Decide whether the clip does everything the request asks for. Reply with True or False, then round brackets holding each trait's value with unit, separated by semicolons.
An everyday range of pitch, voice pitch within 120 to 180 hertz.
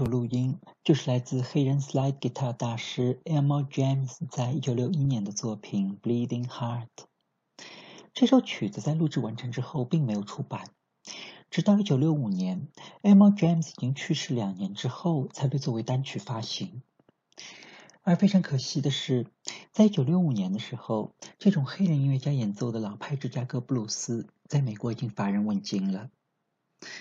True (5.0 semitones; 135 Hz)